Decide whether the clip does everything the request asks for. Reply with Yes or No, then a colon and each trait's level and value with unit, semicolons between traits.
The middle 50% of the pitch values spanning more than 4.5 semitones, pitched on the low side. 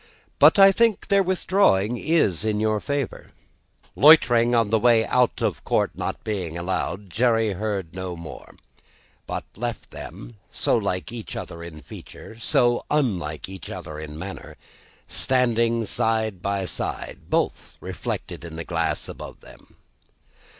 Yes: average, 5.0 semitones; low, 110 Hz